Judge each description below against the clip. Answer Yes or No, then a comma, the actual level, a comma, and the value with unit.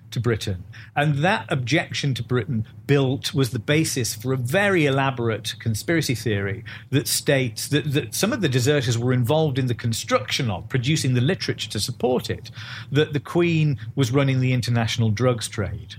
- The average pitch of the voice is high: No, low, 125 Hz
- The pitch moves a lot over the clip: No, average, 3.9 semitones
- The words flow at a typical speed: Yes, average, 175 wpm